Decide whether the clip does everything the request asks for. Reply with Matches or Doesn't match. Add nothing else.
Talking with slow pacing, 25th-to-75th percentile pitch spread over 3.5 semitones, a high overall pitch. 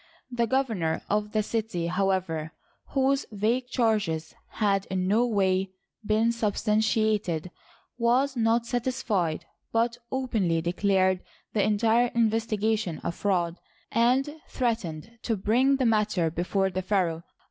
Matches